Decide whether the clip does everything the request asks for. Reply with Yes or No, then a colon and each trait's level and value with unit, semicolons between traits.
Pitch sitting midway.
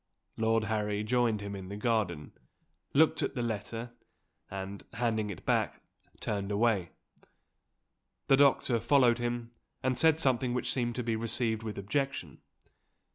No: low, 115 Hz